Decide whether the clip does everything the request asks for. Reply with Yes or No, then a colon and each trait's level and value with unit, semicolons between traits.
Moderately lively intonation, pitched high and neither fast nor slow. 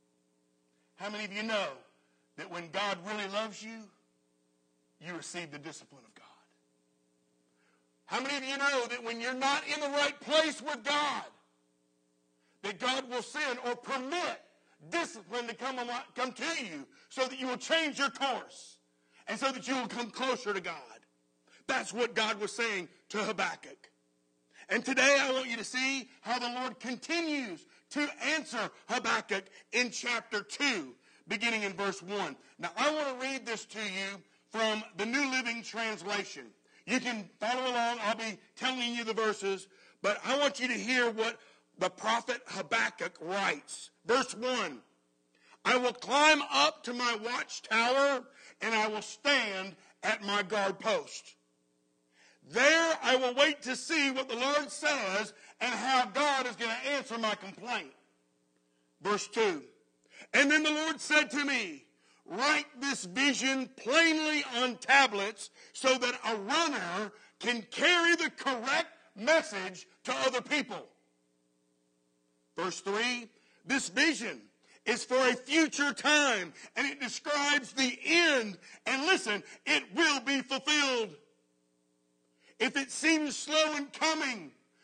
No: wide, 5.9 semitones; high, 240 Hz; average, 150 wpm